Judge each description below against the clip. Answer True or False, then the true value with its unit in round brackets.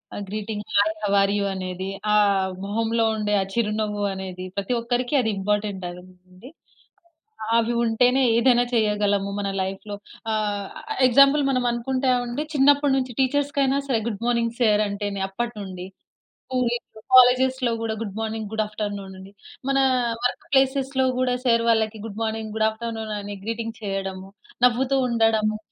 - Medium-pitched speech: False (220 Hz)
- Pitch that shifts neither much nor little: True (3.3 semitones)